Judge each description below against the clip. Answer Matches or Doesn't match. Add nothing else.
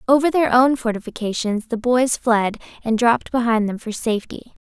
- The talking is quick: Doesn't match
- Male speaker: Doesn't match